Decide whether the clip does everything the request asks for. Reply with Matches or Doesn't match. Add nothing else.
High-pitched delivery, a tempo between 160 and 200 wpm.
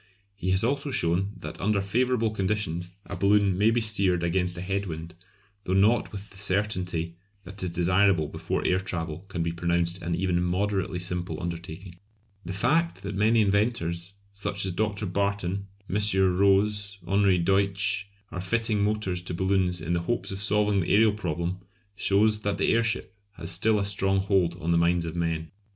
Doesn't match